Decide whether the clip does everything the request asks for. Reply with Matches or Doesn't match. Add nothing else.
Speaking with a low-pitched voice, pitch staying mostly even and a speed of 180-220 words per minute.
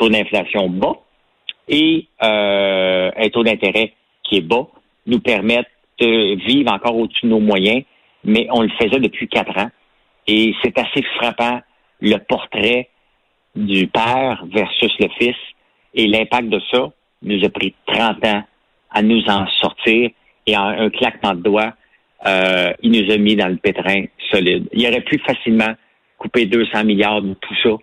Doesn't match